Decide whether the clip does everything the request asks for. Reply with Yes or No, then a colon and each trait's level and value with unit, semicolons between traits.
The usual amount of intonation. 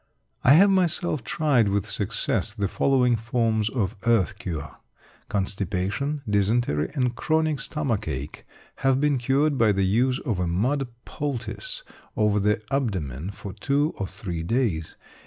No: wide, 5.9 semitones